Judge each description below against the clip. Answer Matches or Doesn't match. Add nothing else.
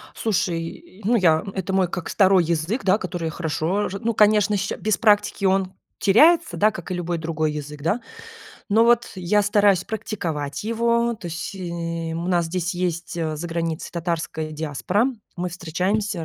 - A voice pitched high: Doesn't match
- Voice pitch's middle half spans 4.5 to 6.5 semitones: Doesn't match